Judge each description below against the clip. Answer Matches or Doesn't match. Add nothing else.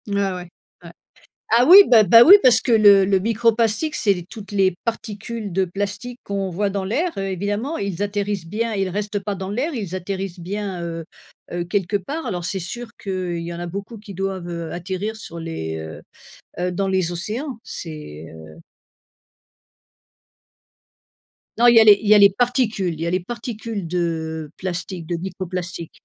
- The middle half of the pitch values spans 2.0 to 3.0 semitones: Doesn't match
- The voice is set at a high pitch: Matches